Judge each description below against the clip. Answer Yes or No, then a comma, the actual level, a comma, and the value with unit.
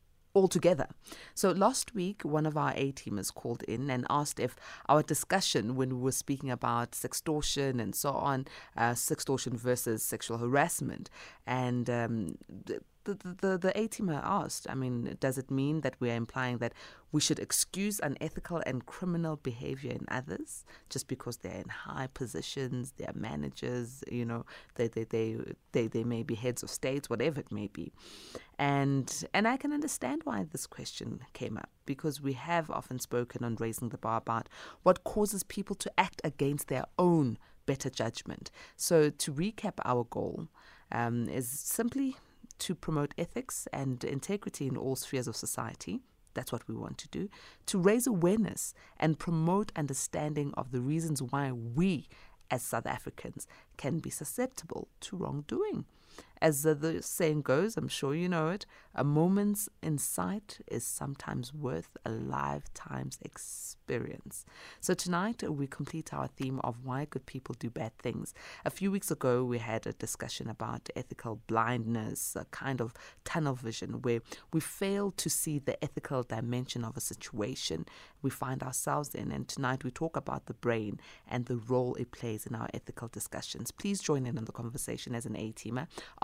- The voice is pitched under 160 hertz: Yes, low, 135 Hz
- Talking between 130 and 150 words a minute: No, average, 170 wpm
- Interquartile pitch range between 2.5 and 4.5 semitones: No, average, 5.2 semitones